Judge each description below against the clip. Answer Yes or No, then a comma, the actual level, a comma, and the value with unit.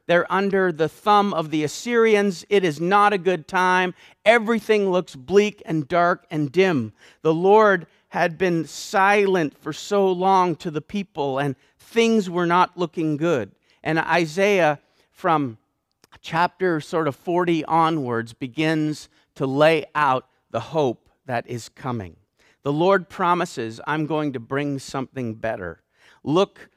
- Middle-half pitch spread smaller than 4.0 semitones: No, average, 4.7 semitones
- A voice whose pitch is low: No, medium, 165 Hz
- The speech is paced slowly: No, average, 145 wpm